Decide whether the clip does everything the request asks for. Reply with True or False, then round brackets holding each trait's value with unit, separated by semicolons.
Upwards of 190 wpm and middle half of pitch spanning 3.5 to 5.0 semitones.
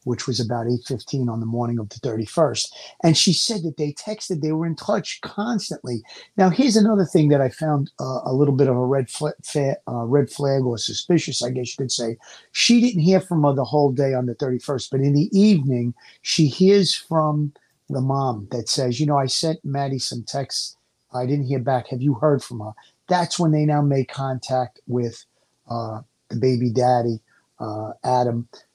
True (205 wpm; 4.1 semitones)